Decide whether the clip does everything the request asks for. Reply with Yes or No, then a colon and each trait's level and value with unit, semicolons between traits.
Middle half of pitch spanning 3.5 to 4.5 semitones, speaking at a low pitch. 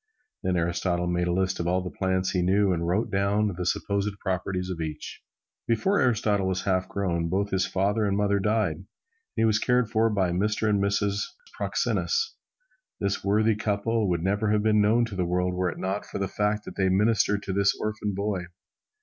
No: narrow, 2.4 semitones; low, 100 Hz